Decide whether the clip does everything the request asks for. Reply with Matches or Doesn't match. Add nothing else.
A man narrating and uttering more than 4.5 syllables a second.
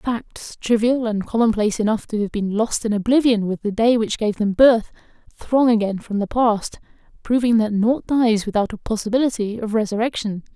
Doesn't match